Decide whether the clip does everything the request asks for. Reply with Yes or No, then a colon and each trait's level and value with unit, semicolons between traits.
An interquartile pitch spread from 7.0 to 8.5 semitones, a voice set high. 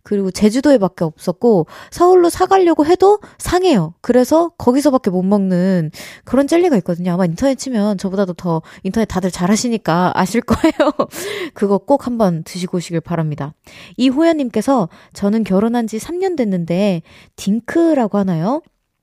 Yes: wide, 7.5 semitones; high, 215 Hz